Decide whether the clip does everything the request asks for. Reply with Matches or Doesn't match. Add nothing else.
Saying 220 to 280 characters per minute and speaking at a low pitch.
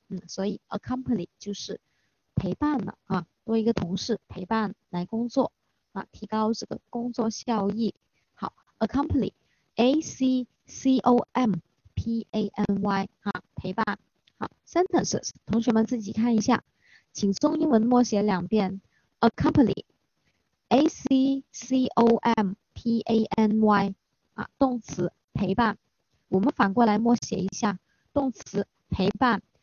Doesn't match